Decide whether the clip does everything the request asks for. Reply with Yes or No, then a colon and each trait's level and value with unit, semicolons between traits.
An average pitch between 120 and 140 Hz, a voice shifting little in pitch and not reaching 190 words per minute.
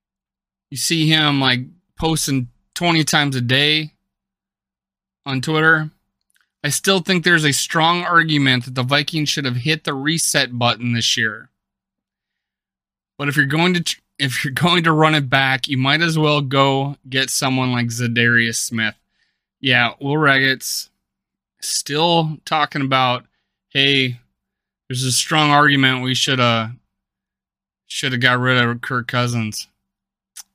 No: low, 135 Hz; average, 3.5 semitones; average, 145 wpm